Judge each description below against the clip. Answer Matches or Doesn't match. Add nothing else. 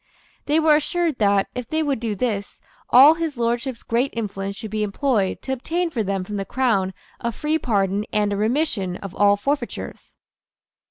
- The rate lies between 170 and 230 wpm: Matches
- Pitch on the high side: Matches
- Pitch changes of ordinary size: Doesn't match